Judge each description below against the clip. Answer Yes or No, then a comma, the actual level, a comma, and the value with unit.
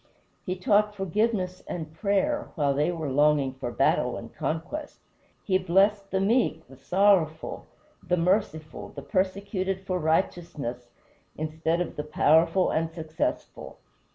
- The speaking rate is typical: No, slow, 130 wpm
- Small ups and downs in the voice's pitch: No, average, 3.8 semitones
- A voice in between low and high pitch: Yes, medium, 175 Hz